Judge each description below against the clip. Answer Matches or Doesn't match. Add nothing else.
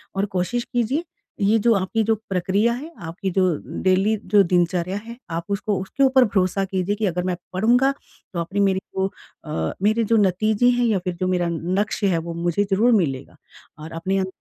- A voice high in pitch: Matches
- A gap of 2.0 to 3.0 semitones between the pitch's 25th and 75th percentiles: Doesn't match